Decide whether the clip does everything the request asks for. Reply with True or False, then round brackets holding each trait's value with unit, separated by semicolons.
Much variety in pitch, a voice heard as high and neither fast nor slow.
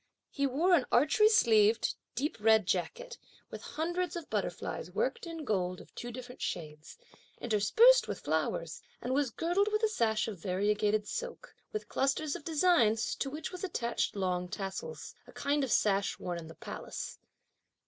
True (8.8 semitones; 255 Hz; 165 wpm)